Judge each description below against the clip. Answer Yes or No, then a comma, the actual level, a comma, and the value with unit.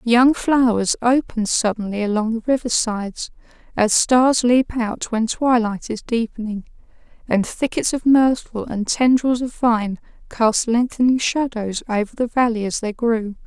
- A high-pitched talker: Yes, high, 230 Hz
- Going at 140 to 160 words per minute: Yes, average, 145 wpm